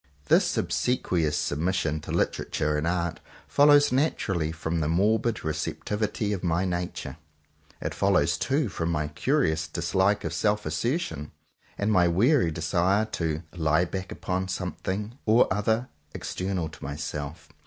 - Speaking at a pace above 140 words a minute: No, slow, 135 wpm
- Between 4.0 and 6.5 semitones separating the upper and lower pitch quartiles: Yes, average, 4.7 semitones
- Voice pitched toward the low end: Yes, very low, 90 Hz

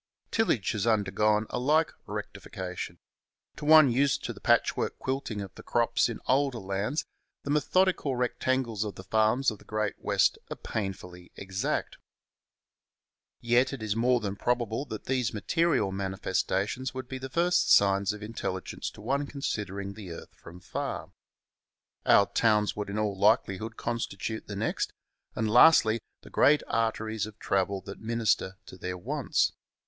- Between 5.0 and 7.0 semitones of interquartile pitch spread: No, average, 4.3 semitones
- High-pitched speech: No, low, 110 Hz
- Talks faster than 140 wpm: Yes, average, 155 wpm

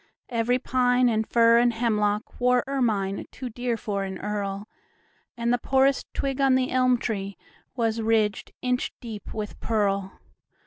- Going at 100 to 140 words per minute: Yes, slow, 135 wpm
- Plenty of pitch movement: No, average, 3.1 semitones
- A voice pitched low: No, high, 230 Hz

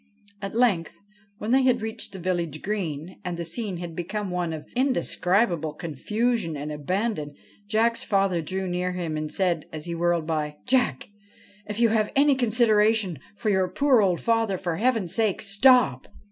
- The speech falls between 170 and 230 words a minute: Yes, average, 175 wpm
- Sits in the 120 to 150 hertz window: No, high, 190 Hz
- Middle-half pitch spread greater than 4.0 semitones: Yes, average, 5.0 semitones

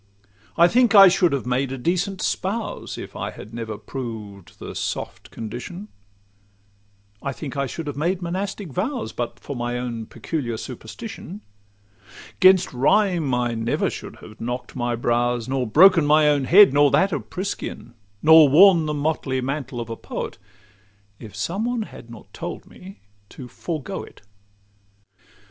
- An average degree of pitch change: No, wide, 7.1 semitones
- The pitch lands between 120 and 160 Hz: Yes, medium, 140 Hz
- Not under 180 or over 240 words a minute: No, average, 160 wpm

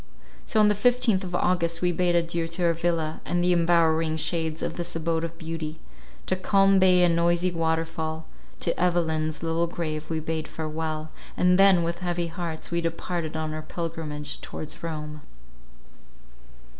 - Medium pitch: Yes, medium, 165 Hz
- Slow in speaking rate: No, average, 165 wpm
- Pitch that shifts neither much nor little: No, narrow, 1.7 semitones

